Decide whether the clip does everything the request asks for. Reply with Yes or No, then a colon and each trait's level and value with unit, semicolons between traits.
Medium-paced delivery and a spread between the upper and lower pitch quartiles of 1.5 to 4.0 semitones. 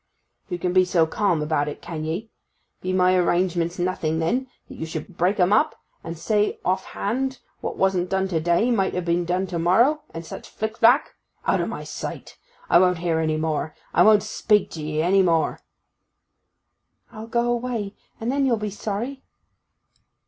No: average, 185 wpm; average, 4.5 semitones